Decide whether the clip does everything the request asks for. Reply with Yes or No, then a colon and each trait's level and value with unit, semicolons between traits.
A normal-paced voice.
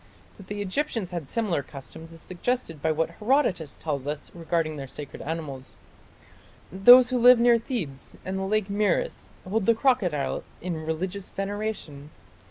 Yes: average, 160 wpm